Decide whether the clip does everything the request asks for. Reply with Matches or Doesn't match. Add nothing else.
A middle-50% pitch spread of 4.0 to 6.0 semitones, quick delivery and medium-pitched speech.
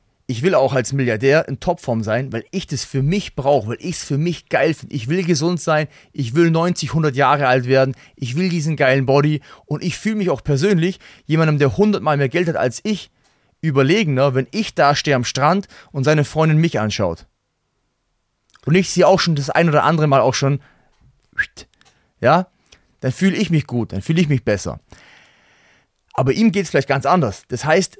Matches